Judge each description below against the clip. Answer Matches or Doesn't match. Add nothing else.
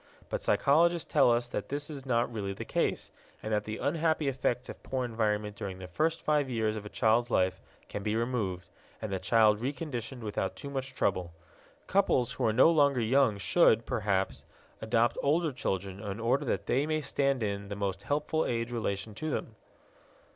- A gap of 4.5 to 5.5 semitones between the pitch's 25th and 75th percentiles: Matches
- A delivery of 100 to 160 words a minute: Doesn't match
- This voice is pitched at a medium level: Doesn't match